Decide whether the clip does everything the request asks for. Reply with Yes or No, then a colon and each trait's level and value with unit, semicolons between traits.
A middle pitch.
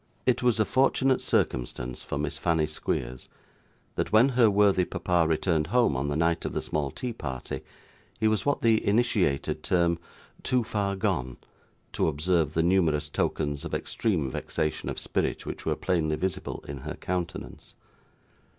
No: very low, 85 Hz